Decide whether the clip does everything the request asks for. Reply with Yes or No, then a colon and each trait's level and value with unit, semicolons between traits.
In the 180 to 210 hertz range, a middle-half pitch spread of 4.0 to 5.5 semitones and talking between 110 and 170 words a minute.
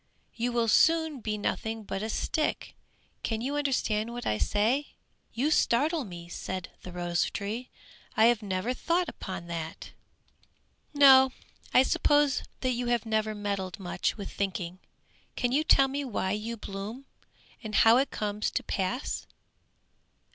No: high, 225 Hz; average, 4.8 semitones; average, 150 wpm